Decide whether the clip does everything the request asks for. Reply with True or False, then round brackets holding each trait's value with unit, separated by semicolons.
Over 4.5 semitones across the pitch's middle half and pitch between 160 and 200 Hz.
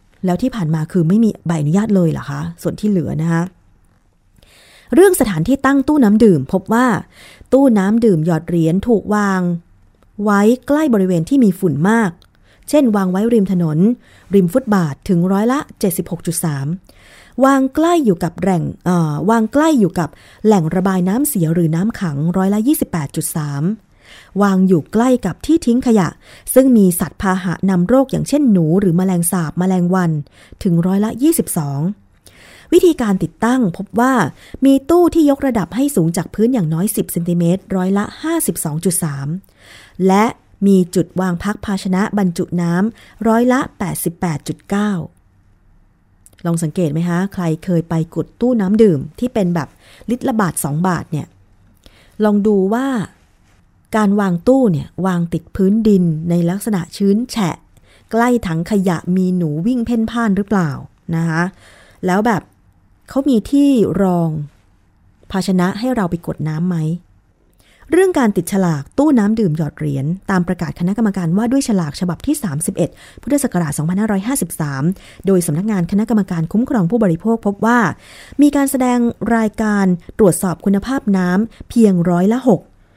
True (5.0 semitones; 190 Hz)